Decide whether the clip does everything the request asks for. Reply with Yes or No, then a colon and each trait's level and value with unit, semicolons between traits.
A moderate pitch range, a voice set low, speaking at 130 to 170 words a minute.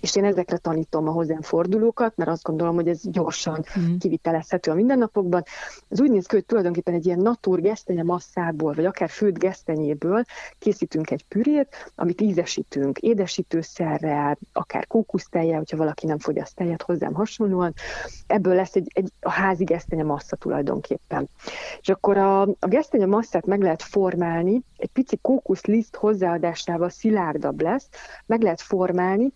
No: average, 4.0 semitones; medium, 185 Hz; average, 150 wpm